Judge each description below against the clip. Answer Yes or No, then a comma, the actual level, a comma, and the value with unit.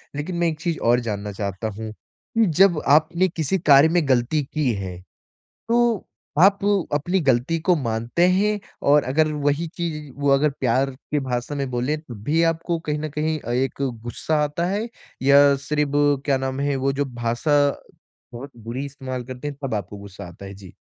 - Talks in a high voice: No, medium, 140 Hz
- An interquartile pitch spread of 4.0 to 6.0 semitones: Yes, average, 4.5 semitones